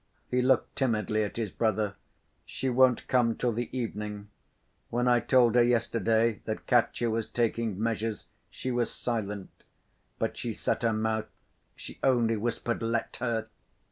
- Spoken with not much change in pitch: Yes, narrow, 1.8 semitones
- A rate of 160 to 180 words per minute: No, average, 150 wpm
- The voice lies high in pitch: No, low, 115 Hz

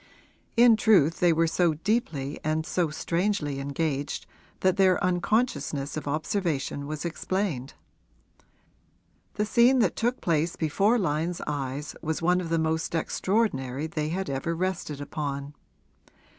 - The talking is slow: Yes, slow, 130 wpm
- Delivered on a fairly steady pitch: No, average, 4.2 semitones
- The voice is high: No, medium, 165 Hz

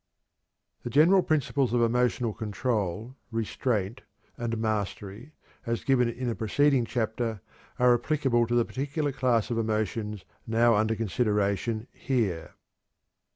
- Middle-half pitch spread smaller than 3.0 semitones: Yes, narrow, 2.6 semitones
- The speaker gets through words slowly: Yes, slow, 120 wpm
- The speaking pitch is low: Yes, low, 115 Hz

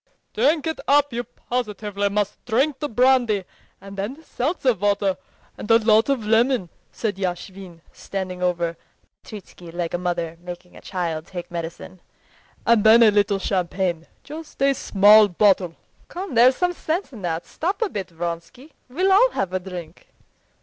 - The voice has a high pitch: Yes, high, 205 Hz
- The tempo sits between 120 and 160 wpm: Yes, average, 155 wpm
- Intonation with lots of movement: Yes, wide, 6.0 semitones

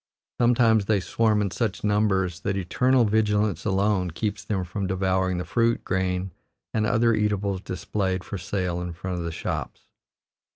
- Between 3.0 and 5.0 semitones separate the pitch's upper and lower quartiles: No, narrow, 2.6 semitones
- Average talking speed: Yes, average, 160 wpm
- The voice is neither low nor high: No, low, 100 Hz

